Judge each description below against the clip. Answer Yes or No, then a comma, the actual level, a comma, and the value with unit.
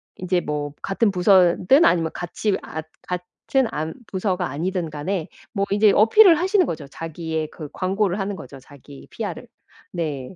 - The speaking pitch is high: No, medium, 180 Hz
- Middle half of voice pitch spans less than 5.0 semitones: Yes, average, 4.2 semitones